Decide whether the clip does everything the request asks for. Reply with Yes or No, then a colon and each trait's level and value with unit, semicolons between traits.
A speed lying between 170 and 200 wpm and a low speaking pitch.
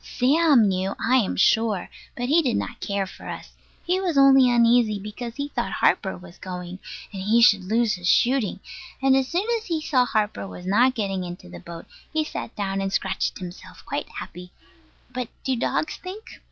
No: average, 195 wpm; high, 230 Hz